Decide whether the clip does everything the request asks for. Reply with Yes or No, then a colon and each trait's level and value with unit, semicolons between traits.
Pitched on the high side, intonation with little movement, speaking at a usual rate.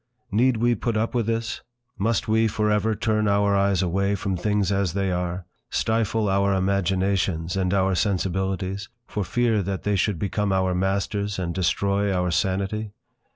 No: low, 100 Hz; narrow, 2.0 semitones; average, 165 wpm